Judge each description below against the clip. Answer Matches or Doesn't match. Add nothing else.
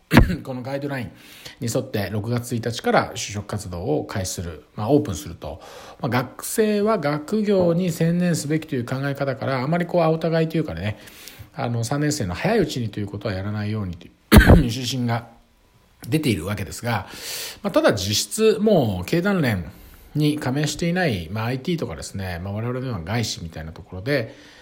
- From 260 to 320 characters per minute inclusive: Doesn't match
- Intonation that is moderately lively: Doesn't match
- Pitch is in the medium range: Doesn't match